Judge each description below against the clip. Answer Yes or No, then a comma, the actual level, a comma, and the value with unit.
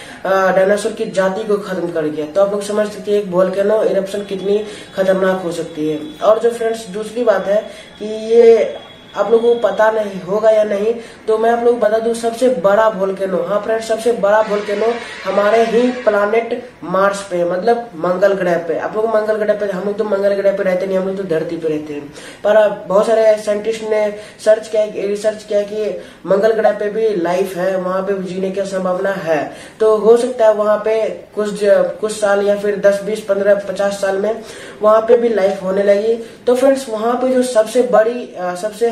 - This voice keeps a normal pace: No, fast, 215 wpm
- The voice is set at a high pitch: Yes, high, 210 Hz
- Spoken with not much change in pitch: Yes, narrow, 2.3 semitones